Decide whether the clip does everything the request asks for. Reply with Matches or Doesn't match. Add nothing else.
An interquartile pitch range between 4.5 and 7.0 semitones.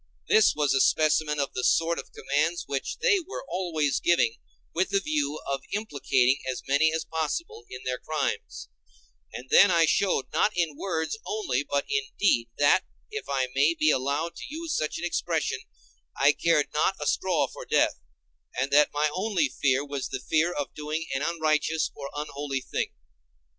Doesn't match